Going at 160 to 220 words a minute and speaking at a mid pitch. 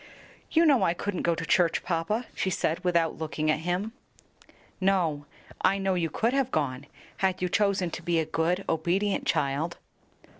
Yes: average, 175 wpm; medium, 175 Hz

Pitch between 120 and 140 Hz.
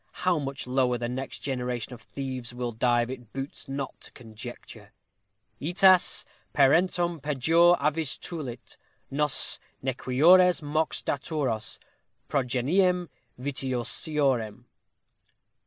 Yes: low, 135 Hz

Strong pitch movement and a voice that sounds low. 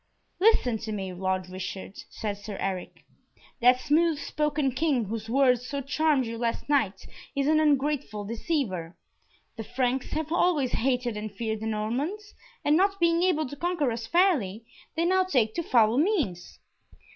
No: wide, 6.2 semitones; very high, 255 Hz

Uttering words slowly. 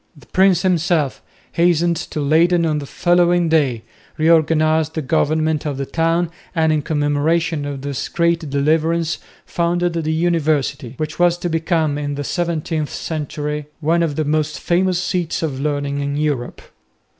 No: average, 155 wpm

